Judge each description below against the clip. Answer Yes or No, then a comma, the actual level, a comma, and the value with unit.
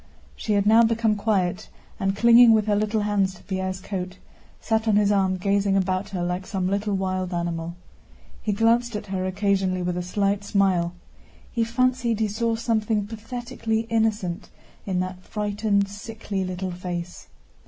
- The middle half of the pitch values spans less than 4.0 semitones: Yes, average, 2.9 semitones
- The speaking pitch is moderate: No, high, 200 Hz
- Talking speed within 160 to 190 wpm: Yes, average, 165 wpm